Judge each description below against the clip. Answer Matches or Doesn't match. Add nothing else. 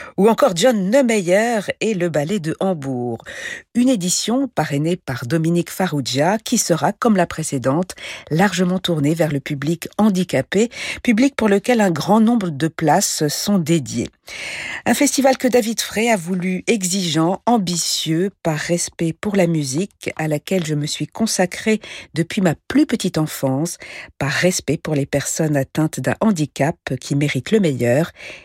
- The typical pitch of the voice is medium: Matches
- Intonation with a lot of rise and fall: Matches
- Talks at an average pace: Matches